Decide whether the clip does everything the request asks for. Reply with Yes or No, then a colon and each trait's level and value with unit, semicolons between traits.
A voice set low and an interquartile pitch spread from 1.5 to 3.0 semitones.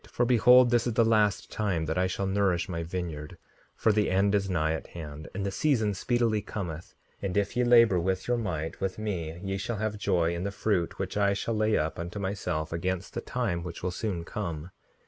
No: very low, 95 Hz; average, 4.0 semitones